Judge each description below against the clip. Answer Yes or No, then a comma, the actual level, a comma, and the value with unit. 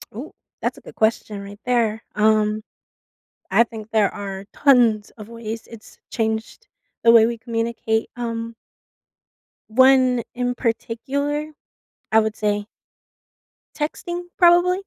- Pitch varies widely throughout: No, narrow, 2.5 semitones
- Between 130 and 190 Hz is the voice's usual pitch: No, high, 230 Hz